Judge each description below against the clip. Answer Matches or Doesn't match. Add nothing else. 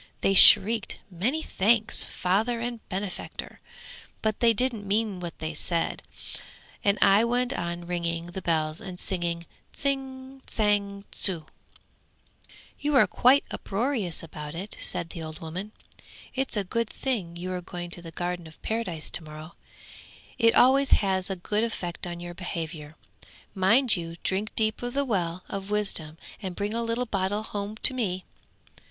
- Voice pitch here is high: Matches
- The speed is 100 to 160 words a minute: Matches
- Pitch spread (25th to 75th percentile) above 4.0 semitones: Matches